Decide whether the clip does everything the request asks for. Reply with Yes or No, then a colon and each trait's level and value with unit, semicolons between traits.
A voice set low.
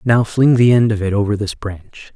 Yes: low, 110 Hz